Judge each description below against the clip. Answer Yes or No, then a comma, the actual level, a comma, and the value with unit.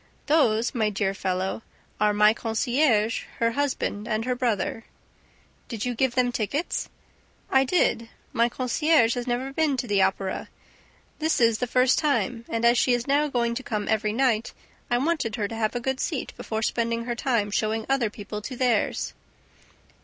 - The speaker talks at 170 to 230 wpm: Yes, average, 180 wpm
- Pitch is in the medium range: No, high, 235 Hz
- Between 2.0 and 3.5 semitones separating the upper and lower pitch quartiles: Yes, average, 3.0 semitones